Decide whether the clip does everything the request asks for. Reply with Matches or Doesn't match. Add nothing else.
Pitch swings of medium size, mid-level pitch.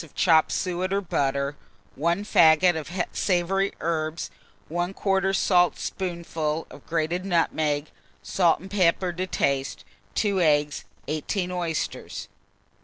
Matches